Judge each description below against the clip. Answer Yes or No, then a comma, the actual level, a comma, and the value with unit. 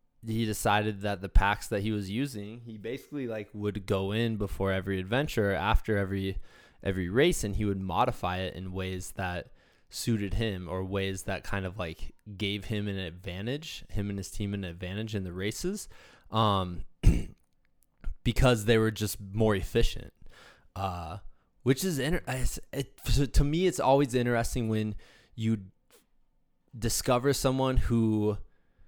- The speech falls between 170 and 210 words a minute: No, average, 155 wpm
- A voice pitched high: No, low, 105 Hz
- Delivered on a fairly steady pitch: No, average, 3.4 semitones